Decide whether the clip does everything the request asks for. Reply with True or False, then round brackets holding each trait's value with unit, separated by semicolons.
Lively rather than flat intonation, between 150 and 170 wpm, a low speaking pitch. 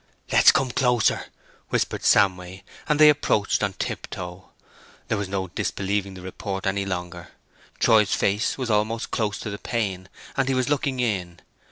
False (3.8 semitones; 160 wpm; 100 Hz)